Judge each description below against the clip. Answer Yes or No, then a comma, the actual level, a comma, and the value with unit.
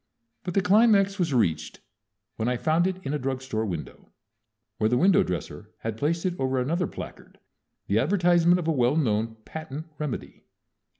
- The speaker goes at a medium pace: Yes, average, 175 wpm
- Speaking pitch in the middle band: Yes, medium, 150 Hz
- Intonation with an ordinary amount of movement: No, wide, 6.5 semitones